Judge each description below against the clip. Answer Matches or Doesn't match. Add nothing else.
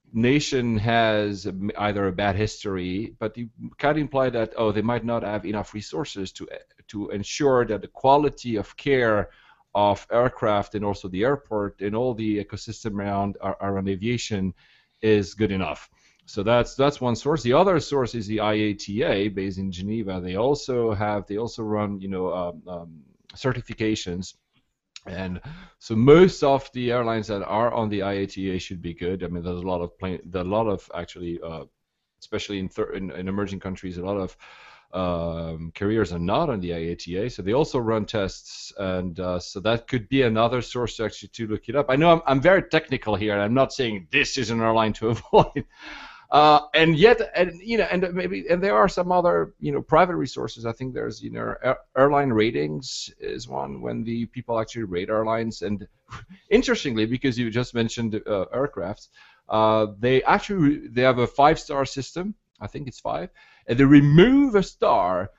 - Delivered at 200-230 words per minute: Doesn't match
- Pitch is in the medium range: Doesn't match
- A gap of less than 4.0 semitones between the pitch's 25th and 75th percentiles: Doesn't match